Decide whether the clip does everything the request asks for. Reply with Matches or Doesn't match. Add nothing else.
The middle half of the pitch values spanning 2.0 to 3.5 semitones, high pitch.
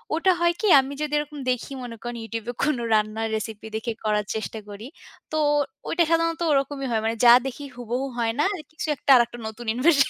Doesn't match